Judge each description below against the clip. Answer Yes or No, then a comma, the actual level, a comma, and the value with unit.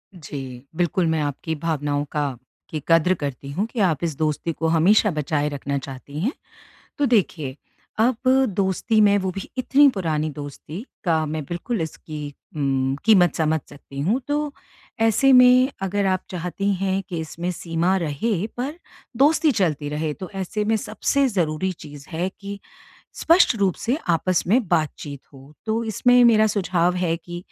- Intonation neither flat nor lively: No, wide, 5.8 semitones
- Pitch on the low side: No, medium, 175 Hz